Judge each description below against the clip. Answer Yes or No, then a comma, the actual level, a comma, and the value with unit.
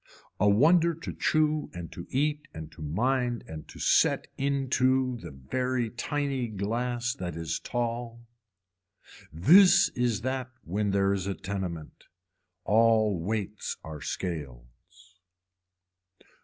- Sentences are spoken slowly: Yes, slow, 120 wpm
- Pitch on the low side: Yes, low, 110 Hz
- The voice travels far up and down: Yes, wide, 6.4 semitones